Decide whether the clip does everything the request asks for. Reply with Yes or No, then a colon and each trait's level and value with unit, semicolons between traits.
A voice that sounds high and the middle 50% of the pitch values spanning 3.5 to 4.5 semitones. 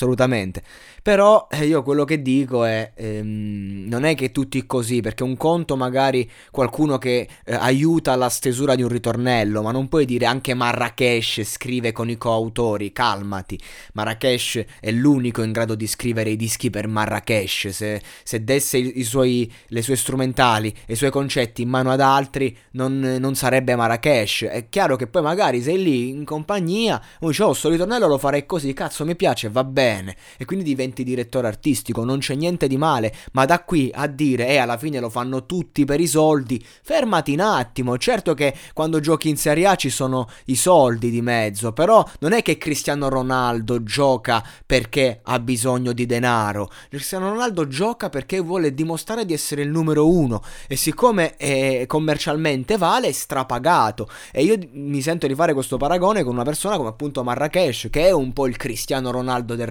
No: low, 130 Hz; average, 4.0 semitones